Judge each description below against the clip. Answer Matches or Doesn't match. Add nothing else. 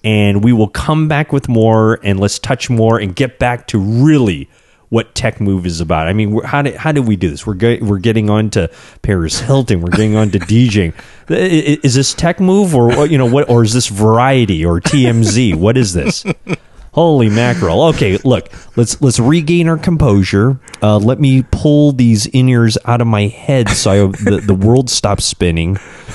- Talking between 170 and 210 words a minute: Matches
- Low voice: Matches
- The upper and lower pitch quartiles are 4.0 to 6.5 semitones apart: Matches